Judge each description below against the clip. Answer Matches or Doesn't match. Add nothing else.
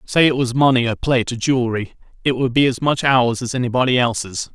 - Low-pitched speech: Matches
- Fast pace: Matches